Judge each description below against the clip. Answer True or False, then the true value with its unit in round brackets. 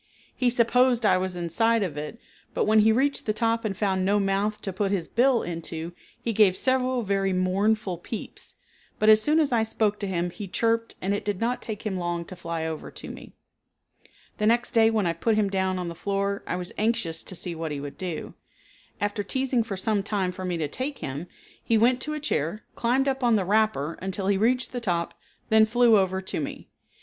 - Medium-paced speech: False (220 wpm)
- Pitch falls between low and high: False (205 Hz)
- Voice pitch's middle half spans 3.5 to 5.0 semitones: True (3.9 semitones)